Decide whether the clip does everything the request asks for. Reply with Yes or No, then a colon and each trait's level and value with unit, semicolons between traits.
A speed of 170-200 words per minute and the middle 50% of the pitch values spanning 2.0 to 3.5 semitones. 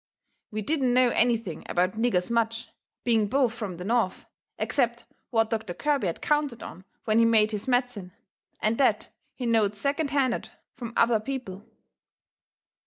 No: average, 155 wpm; average, 2.8 semitones